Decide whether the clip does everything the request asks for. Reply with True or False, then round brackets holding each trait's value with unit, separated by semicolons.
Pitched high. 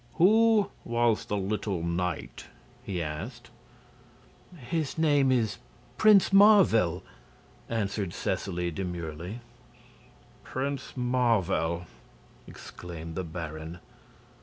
False (105 Hz)